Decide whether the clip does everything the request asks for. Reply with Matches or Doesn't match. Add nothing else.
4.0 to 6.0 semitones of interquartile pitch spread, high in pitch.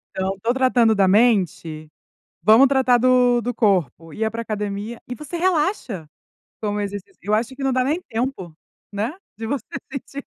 Matches